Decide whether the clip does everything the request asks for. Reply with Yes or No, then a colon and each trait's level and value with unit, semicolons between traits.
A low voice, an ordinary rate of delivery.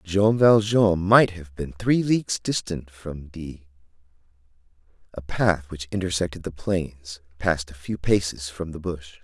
Yes: very low, 85 Hz; average, 150 wpm